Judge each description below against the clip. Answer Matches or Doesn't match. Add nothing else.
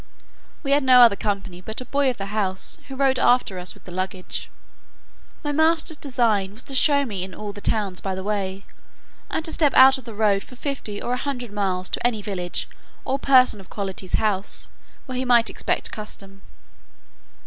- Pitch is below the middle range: Doesn't match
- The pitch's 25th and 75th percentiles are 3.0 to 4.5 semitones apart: Doesn't match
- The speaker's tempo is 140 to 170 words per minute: Doesn't match